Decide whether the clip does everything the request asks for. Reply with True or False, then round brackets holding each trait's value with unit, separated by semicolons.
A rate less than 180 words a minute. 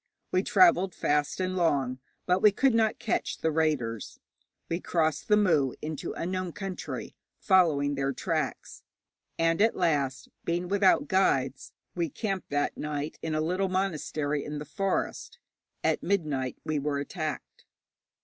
True (145 wpm)